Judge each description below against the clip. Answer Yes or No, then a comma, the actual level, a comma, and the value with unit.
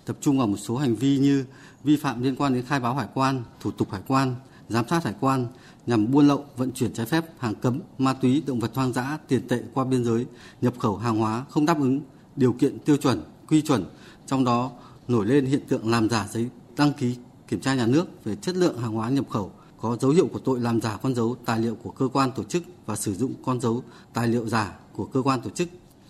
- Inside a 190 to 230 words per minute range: No, fast, 250 wpm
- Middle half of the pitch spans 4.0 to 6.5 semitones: No, average, 3.2 semitones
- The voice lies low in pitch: Yes, low, 130 Hz